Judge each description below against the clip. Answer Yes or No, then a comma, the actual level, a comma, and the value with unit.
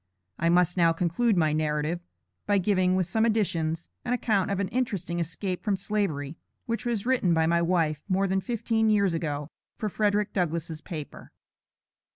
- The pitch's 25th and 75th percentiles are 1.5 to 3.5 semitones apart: No, average, 4.1 semitones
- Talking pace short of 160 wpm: No, average, 170 wpm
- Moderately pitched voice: Yes, medium, 180 Hz